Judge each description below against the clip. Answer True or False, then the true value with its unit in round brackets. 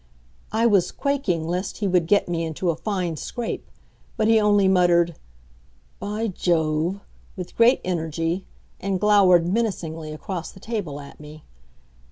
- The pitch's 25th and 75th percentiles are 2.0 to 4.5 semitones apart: True (3.9 semitones)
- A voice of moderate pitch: True (180 Hz)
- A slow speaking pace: False (145 wpm)